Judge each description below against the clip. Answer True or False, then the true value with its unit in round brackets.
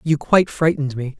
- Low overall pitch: False (150 Hz)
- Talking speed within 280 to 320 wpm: False (200 wpm)